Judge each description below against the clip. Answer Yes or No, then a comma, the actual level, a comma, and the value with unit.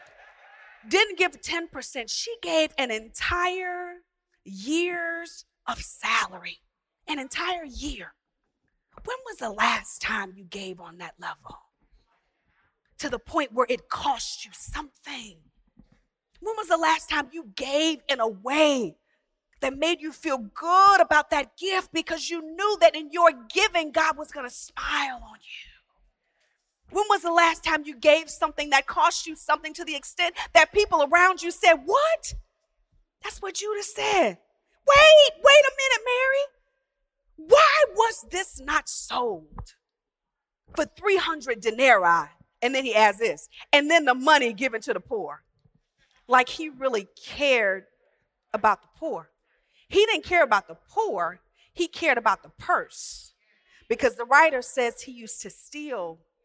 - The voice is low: No, very high, 310 Hz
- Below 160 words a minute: Yes, average, 150 wpm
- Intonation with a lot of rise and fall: No, average, 4.7 semitones